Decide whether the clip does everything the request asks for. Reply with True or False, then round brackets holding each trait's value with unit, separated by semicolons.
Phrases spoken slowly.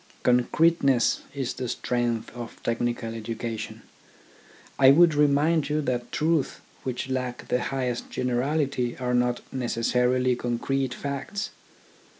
True (120 wpm)